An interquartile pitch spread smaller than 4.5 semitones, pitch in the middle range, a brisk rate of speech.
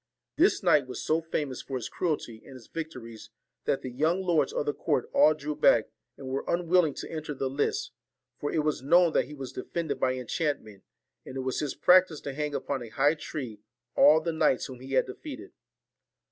Yes: average, 3.8 semitones; medium, 145 Hz; fast, 210 wpm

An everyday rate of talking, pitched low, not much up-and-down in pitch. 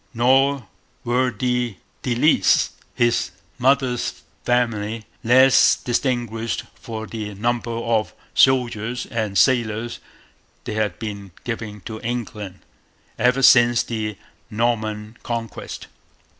No: slow, 100 wpm; low, 115 Hz; narrow, 2.2 semitones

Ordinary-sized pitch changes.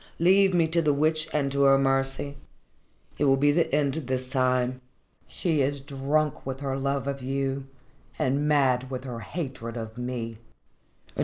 No: narrow, 2.2 semitones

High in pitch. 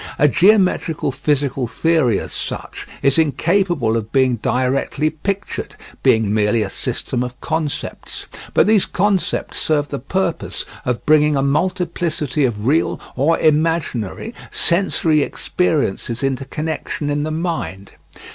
No: medium, 150 Hz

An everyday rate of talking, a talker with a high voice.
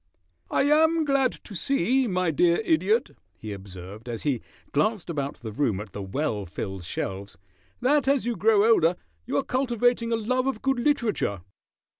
Yes: average, 170 wpm; high, 195 Hz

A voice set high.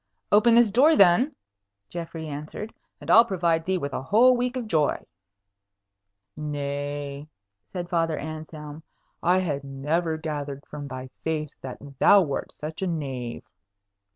No: medium, 155 Hz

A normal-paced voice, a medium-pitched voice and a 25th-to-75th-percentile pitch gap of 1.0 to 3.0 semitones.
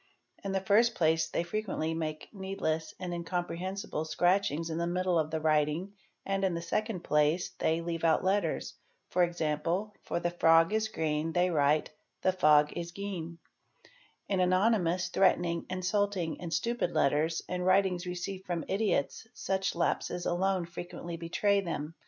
Yes: average, 150 wpm; medium, 175 Hz; average, 2.7 semitones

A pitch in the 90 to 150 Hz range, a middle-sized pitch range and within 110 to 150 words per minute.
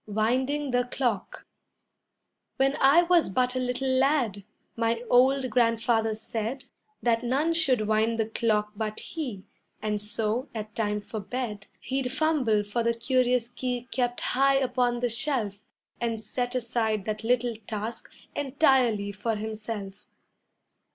No: high, 235 Hz; average, 3.1 semitones; average, 140 wpm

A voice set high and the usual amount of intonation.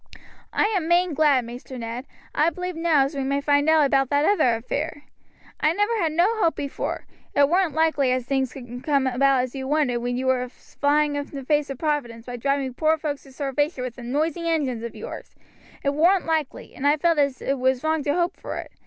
Yes: very high, 285 Hz; average, 3.3 semitones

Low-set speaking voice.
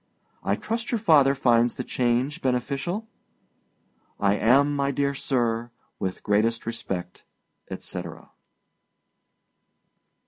Yes: low, 125 Hz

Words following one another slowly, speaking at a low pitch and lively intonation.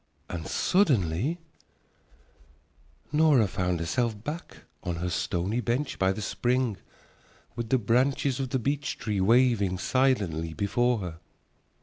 Yes: slow, 120 wpm; low, 115 Hz; wide, 5.9 semitones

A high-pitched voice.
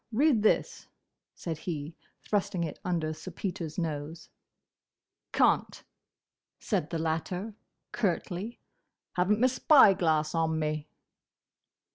No: medium, 170 Hz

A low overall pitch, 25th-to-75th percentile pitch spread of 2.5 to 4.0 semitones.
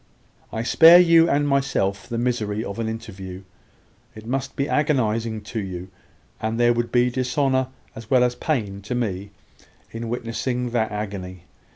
Yes: low, 115 Hz; average, 3.6 semitones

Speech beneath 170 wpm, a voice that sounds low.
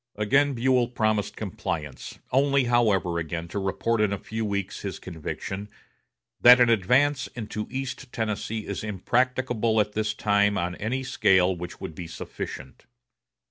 Yes: average, 145 wpm; low, 105 Hz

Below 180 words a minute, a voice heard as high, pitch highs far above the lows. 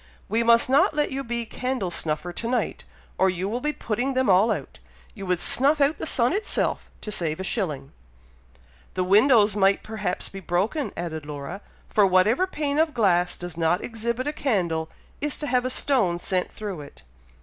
No: average, 190 wpm; high, 210 Hz; wide, 6.2 semitones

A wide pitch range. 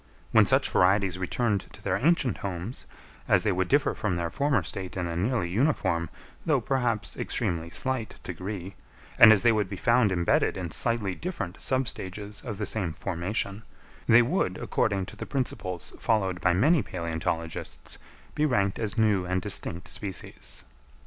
No: average, 4.4 semitones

